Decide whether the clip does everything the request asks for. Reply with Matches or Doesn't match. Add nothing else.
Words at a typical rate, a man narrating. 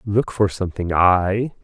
Matches